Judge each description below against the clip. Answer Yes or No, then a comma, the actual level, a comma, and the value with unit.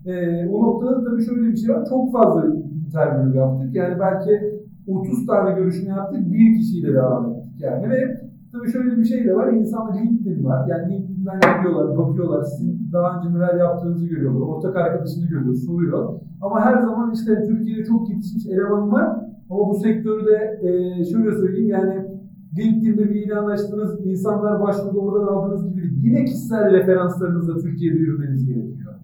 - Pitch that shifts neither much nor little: Yes, average, 4.0 semitones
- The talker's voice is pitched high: Yes, high, 195 Hz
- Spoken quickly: Yes, fast, 165 wpm